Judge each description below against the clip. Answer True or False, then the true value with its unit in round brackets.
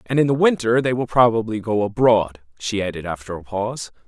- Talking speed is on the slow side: False (205 wpm)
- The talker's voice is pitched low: True (115 Hz)